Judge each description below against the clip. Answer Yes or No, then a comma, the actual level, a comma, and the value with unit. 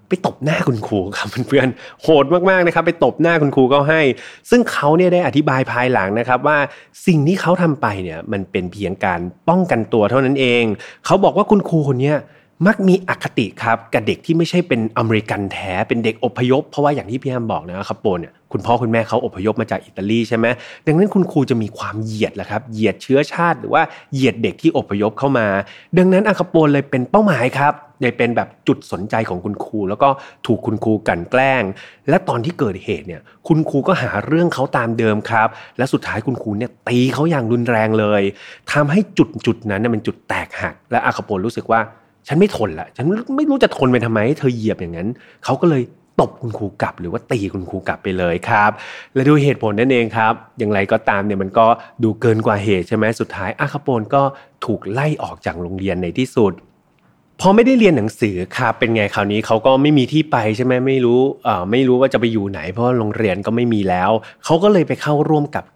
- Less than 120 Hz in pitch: No, low, 125 Hz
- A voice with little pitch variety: No, wide, 5.4 semitones